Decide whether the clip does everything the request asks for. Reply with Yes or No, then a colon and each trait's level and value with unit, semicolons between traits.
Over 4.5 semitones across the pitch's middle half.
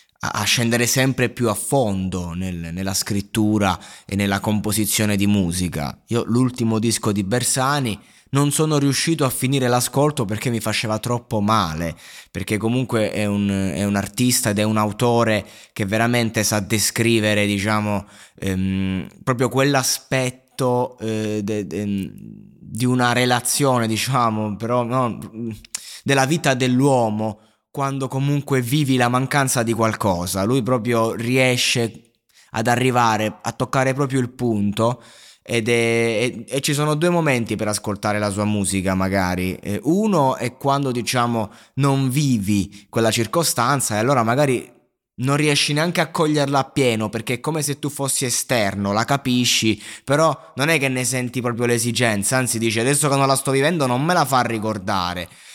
No: average, 3.8 semitones